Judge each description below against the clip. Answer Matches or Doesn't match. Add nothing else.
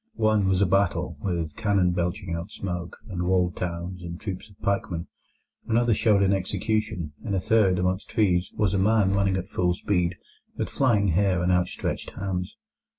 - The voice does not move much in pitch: Matches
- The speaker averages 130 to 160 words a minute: Doesn't match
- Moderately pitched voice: Doesn't match